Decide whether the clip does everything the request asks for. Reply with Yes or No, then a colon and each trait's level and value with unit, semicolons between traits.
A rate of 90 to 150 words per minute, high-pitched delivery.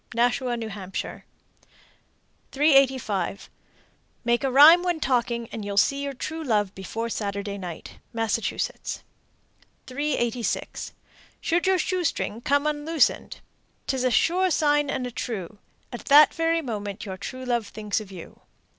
Yes: slow, 135 wpm; high, 245 Hz